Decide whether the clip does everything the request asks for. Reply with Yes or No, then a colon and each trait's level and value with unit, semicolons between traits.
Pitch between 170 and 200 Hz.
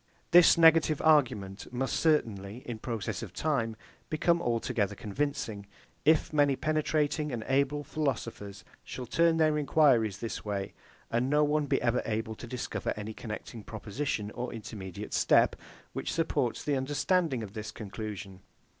No: low, 125 Hz